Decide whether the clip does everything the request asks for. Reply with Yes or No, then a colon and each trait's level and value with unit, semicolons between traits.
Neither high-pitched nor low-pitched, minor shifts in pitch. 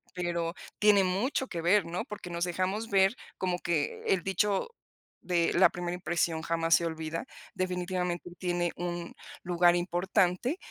Yes: medium, 175 Hz; narrow, 1.6 semitones